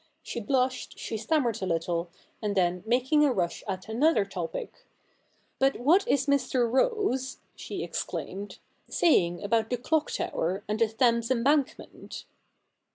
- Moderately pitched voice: No, high, 235 Hz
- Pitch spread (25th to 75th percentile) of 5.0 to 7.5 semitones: Yes, average, 5.3 semitones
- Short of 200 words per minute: Yes, average, 155 wpm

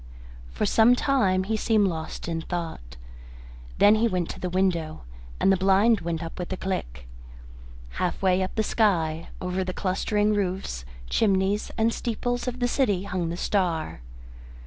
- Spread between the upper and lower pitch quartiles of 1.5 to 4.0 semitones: Yes, average, 3.7 semitones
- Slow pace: No, average, 165 wpm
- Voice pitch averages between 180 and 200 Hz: Yes, high, 190 Hz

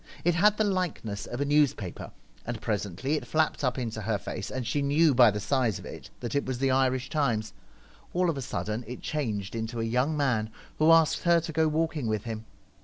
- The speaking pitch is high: No, low, 130 Hz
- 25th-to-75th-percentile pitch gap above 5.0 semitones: Yes, wide, 5.5 semitones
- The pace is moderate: No, fast, 225 wpm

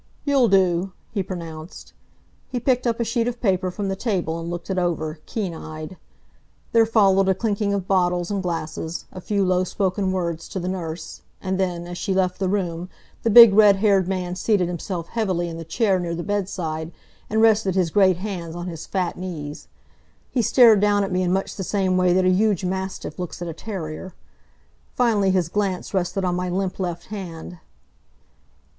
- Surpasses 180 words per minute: Yes, average, 195 wpm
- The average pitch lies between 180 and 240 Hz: Yes, medium, 185 Hz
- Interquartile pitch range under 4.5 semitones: Yes, narrow, 2.5 semitones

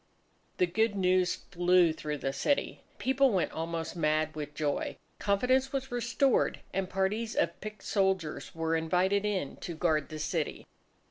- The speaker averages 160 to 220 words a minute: No, average, 150 wpm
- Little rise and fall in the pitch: No, average, 4.7 semitones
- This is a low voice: No, medium, 180 Hz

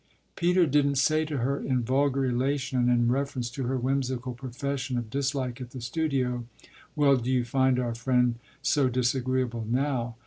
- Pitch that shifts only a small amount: Yes, narrow, 2.1 semitones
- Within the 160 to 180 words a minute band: Yes, average, 170 wpm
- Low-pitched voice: Yes, low, 130 Hz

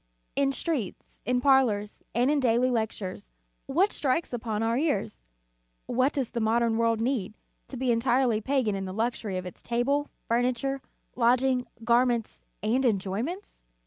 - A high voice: Yes, high, 240 Hz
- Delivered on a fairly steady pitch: No, average, 3.2 semitones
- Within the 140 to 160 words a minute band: Yes, average, 145 wpm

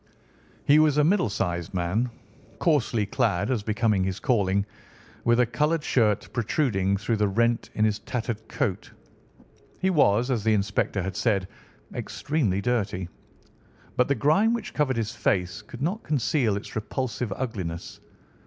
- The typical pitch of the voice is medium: No, low, 115 Hz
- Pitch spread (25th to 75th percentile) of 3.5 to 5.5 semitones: Yes, average, 5.0 semitones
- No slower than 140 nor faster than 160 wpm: Yes, average, 150 wpm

